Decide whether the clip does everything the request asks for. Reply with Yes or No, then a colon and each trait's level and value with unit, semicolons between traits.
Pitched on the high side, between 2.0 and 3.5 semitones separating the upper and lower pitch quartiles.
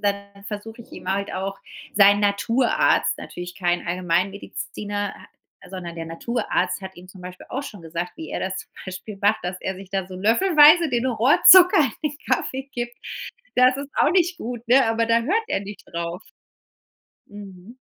No: high, 205 Hz; average, 4.7 semitones